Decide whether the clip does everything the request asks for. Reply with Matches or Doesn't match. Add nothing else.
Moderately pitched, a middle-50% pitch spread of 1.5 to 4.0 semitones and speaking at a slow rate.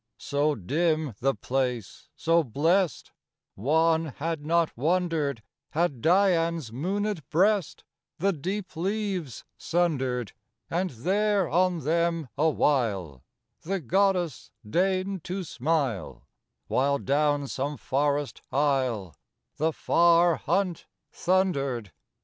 Doesn't match